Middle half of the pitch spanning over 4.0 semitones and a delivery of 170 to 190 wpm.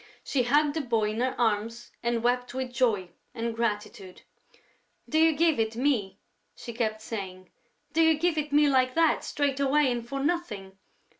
Yes: average, 4.7 semitones; average, 175 wpm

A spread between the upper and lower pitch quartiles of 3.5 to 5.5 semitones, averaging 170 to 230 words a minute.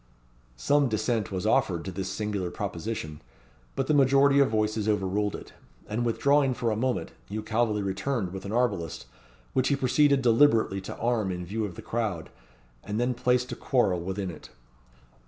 Yes: average, 4.5 semitones; average, 175 wpm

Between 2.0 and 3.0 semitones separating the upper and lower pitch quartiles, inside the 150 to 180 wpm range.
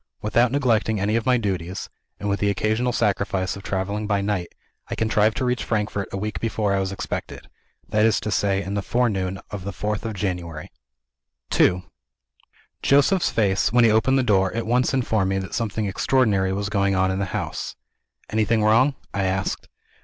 No: average, 2.7 semitones; average, 190 wpm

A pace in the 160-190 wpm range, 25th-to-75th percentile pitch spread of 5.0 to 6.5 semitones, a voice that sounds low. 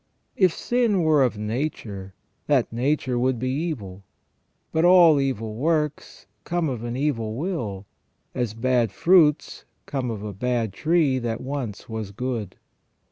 No: average, 145 wpm; wide, 5.4 semitones; low, 130 Hz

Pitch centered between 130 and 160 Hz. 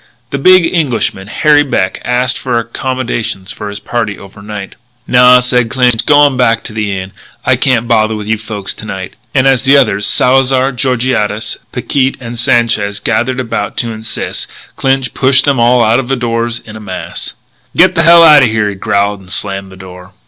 No: low, 115 Hz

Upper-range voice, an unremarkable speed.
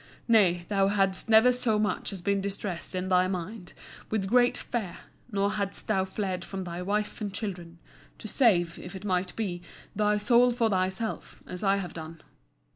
Yes: high, 195 Hz; average, 180 wpm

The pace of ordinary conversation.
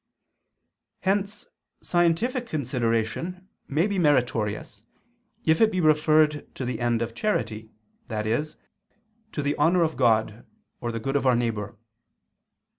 No: slow, 125 wpm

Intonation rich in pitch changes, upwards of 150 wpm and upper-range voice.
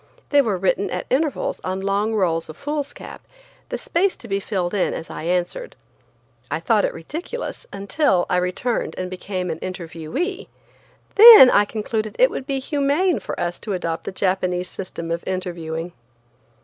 Yes: wide, 7.8 semitones; average, 165 wpm; high, 195 Hz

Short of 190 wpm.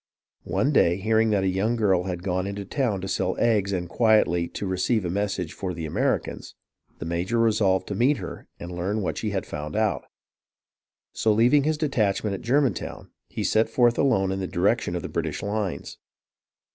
No: average, 195 wpm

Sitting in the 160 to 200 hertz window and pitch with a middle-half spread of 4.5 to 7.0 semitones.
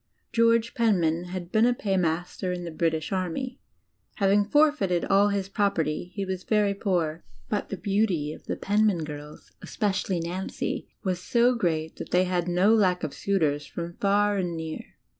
No: medium, 185 Hz; average, 3.5 semitones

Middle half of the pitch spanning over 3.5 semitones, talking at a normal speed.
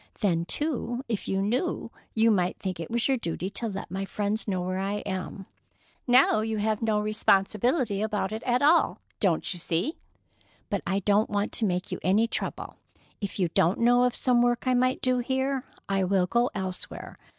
Yes: average, 4.1 semitones; average, 195 wpm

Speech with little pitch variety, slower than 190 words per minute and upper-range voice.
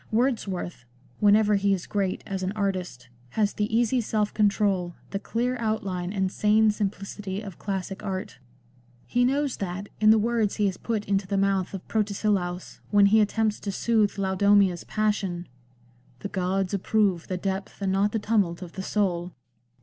Yes: narrow, 2.1 semitones; average, 170 wpm; high, 200 Hz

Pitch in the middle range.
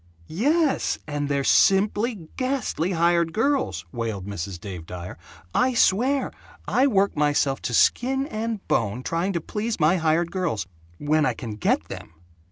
Yes: medium, 170 Hz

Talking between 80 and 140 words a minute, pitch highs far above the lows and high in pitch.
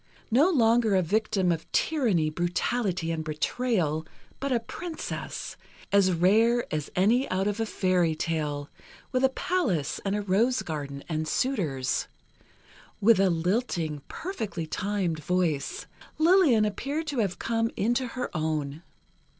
Yes: slow, 135 wpm; wide, 6.8 semitones; high, 195 Hz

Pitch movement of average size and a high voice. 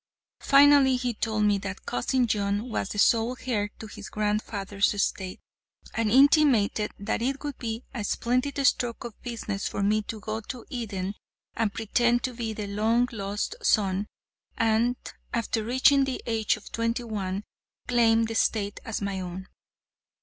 Yes: average, 3.0 semitones; high, 225 Hz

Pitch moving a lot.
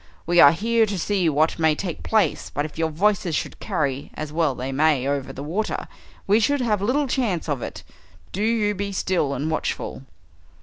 Yes: wide, 5.7 semitones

